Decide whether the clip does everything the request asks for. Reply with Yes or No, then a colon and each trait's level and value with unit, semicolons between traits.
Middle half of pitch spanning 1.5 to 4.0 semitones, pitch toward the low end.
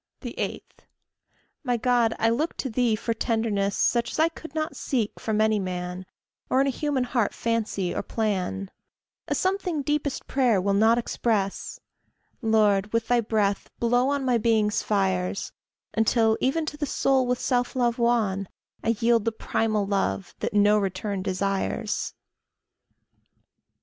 No: average, 3.5 semitones; high, 225 Hz